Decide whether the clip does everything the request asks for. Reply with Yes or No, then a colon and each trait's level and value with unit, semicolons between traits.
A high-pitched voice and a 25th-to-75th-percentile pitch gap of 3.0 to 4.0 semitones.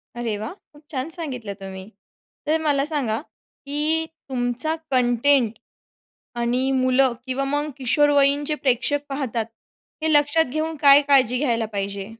Yes: very high, 275 Hz; average, 3.5 semitones